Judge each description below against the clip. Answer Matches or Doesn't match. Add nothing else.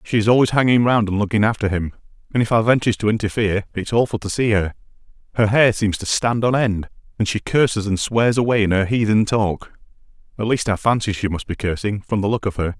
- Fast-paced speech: Matches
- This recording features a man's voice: Matches